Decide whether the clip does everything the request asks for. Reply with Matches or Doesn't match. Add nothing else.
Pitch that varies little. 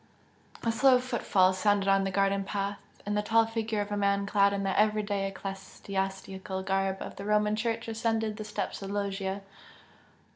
Matches